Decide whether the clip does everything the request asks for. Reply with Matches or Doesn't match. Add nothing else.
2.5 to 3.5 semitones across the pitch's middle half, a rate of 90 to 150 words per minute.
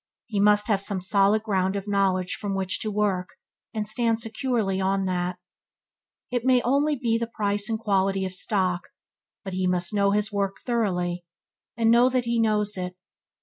Doesn't match